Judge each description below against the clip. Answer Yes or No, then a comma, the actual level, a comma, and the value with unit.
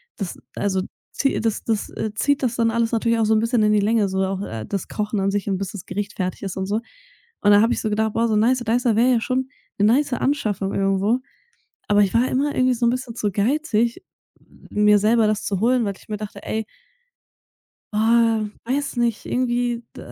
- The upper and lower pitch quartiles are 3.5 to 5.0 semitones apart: No, average, 2.8 semitones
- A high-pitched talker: Yes, high, 220 Hz